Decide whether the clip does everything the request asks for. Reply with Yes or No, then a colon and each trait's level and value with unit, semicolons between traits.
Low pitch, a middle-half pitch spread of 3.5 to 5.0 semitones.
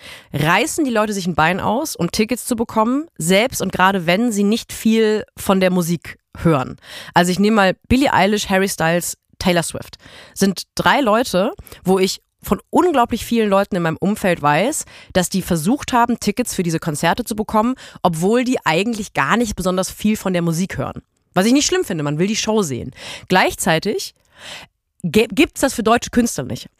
No: high, 200 Hz; average, 4.6 semitones